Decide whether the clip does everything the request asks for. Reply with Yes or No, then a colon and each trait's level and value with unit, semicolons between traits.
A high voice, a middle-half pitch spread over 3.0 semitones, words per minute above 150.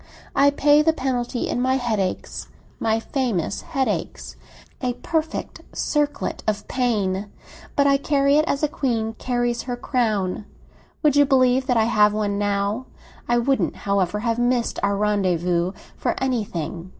No: high, 240 Hz; average, 4.7 semitones; average, 145 wpm